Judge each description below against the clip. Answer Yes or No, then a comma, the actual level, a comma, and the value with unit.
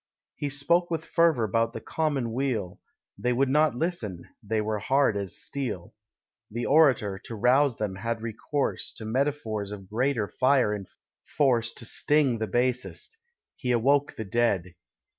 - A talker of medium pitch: No, low, 120 Hz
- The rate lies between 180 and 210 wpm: No, average, 155 wpm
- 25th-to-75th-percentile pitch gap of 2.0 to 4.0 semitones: No, average, 4.5 semitones